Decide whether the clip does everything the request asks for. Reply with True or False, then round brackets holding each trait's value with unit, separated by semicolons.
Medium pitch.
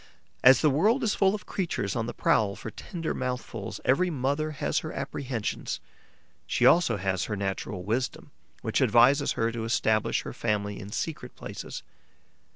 False (125 Hz)